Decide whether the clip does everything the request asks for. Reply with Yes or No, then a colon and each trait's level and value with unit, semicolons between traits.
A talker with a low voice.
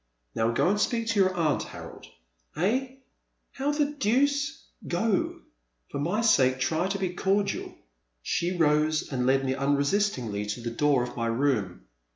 No: medium, 160 Hz